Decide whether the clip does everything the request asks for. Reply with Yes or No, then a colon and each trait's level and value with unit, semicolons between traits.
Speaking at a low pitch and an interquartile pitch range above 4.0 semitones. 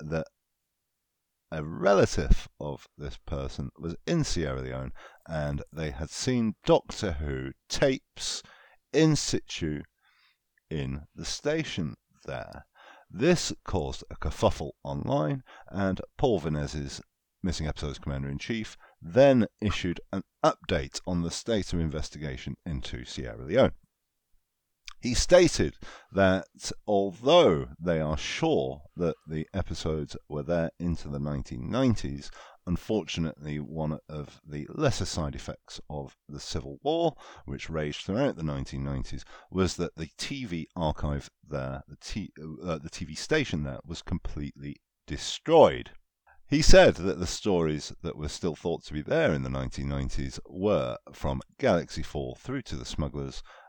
Yes: very low, 80 Hz; average, 4.5 semitones